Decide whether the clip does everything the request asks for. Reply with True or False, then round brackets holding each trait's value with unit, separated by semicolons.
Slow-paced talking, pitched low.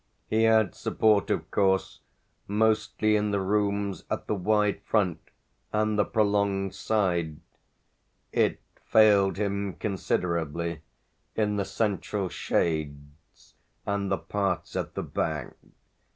True (115 wpm; 100 Hz)